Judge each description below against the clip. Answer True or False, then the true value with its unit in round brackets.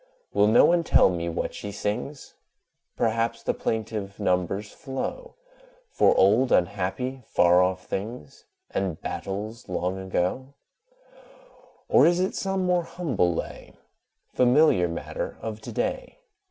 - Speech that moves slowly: True (125 wpm)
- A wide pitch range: True (6.3 semitones)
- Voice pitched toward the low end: True (105 Hz)